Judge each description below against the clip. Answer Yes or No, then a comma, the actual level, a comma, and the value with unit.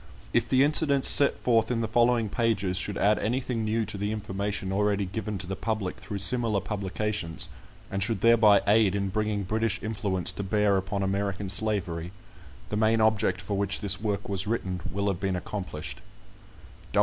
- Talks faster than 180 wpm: No, average, 175 wpm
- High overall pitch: No, low, 105 Hz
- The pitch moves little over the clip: Yes, narrow, 2.3 semitones